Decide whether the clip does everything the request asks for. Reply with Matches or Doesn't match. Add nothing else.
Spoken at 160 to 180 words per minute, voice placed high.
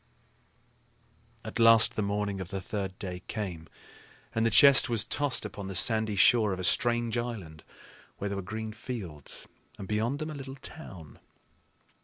Doesn't match